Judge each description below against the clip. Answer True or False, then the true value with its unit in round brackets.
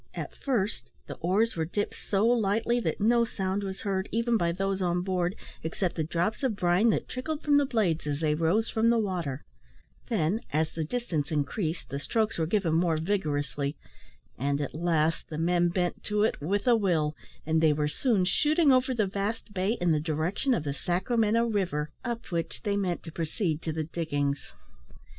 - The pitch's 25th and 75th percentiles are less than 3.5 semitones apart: False (5.6 semitones)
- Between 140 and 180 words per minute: False (195 wpm)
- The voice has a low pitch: False (185 Hz)